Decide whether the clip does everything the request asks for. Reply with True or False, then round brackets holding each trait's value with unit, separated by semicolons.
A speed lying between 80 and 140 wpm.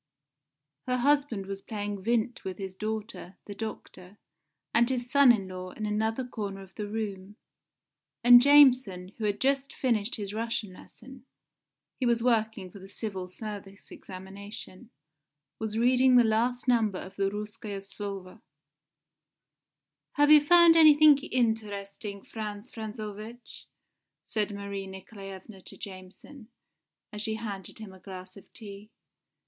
True (135 wpm)